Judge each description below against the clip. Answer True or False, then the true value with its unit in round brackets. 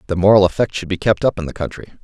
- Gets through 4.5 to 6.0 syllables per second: False (7.3 syllables/s)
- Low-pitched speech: True (95 Hz)